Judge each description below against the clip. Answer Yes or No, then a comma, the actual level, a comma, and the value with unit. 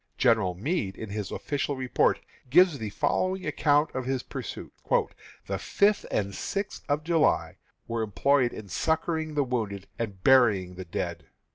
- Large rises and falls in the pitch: Yes, wide, 7.1 semitones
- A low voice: Yes, low, 125 Hz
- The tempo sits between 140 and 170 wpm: Yes, average, 150 wpm